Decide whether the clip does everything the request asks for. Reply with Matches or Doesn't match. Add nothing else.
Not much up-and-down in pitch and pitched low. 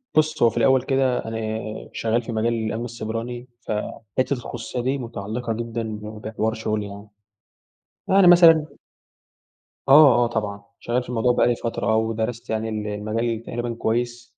Matches